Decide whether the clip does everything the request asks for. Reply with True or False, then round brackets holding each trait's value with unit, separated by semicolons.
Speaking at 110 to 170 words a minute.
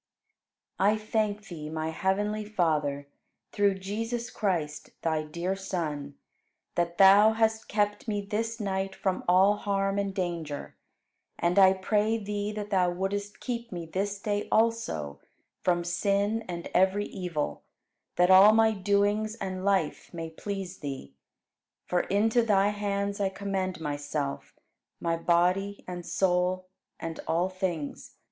True (140 wpm)